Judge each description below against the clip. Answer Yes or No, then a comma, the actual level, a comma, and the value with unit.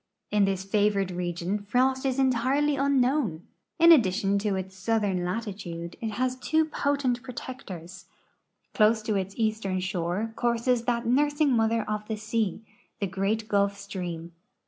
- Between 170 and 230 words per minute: No, average, 145 wpm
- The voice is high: Yes, high, 215 Hz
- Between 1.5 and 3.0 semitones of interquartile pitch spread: No, average, 4.6 semitones